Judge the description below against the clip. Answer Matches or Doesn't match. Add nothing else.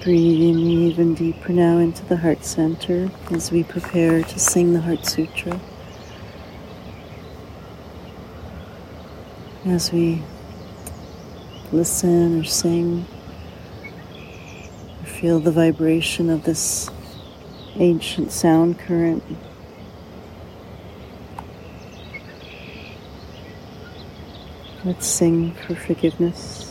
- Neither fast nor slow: Doesn't match